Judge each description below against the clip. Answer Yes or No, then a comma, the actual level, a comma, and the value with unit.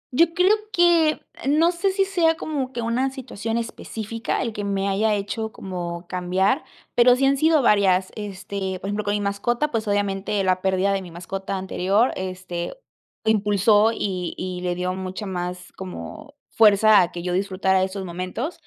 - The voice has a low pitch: No, high, 200 Hz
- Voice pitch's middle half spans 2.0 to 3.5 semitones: No, average, 4.0 semitones